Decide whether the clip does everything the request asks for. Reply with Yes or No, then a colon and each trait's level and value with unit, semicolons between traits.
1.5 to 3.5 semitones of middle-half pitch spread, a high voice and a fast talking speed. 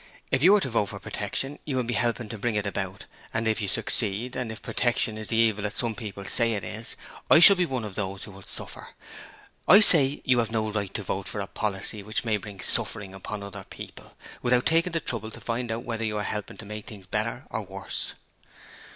No: average, 2.9 semitones; low, 110 Hz; fast, 230 wpm